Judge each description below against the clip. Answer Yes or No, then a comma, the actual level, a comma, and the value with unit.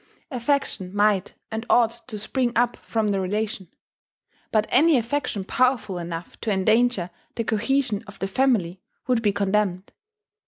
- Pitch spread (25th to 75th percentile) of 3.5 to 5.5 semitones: Yes, average, 3.9 semitones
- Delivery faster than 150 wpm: No, average, 145 wpm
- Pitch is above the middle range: Yes, high, 215 Hz